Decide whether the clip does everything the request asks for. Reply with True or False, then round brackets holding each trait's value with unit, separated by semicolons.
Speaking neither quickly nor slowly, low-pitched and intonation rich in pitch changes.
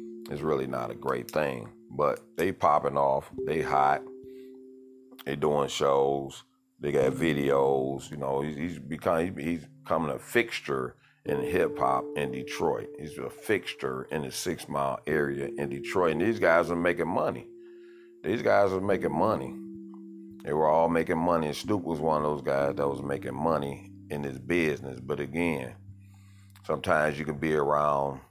True (170 wpm; 75 Hz; 6.0 semitones)